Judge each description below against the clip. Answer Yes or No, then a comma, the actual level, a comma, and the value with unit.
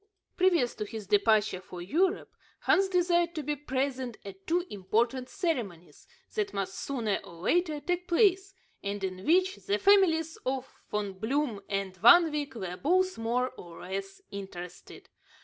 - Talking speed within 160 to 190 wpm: No, average, 150 wpm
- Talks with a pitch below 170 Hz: No, very high, 255 Hz